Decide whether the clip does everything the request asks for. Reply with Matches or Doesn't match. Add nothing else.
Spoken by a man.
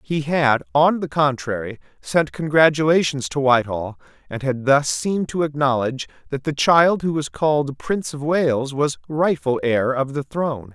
Matches